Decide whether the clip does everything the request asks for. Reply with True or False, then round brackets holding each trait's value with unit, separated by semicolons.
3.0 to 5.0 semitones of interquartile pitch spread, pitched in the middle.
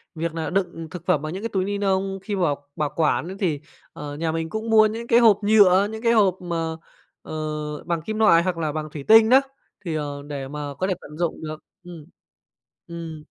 True (4.6 semitones; 175 Hz)